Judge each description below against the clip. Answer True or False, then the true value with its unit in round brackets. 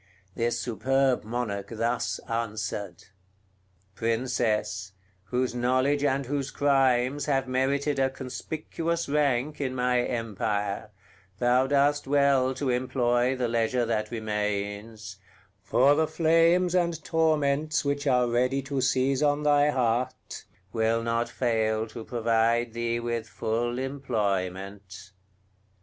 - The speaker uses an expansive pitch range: False (3.6 semitones)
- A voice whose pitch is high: False (125 Hz)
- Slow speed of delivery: True (115 wpm)